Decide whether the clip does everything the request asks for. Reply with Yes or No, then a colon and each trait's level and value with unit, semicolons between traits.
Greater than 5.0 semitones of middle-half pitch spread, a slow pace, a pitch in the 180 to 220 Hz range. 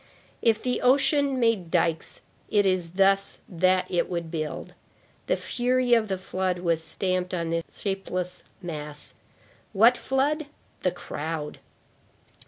Yes: wide, 5.4 semitones; slow, 130 wpm; medium, 185 Hz